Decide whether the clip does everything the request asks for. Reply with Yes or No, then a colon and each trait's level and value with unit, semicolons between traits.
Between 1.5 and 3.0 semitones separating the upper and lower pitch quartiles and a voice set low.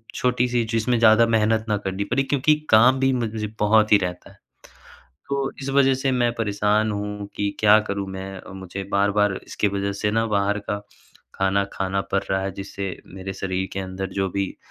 Yes: narrow, 2.6 semitones; low, 105 Hz